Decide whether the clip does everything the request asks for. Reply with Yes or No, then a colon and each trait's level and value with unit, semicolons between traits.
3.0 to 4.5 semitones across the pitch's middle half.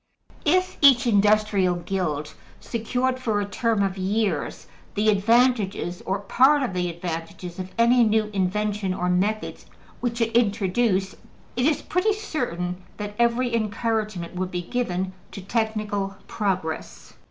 Yes: average, 4.0 semitones